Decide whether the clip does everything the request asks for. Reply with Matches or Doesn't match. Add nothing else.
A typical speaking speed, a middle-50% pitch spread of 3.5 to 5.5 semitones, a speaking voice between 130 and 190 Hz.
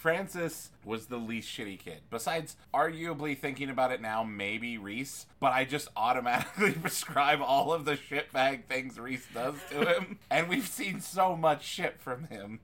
Matches